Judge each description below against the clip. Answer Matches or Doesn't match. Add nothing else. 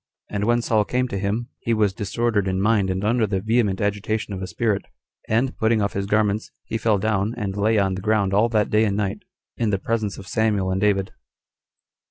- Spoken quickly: Matches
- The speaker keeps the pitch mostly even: Matches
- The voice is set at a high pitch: Doesn't match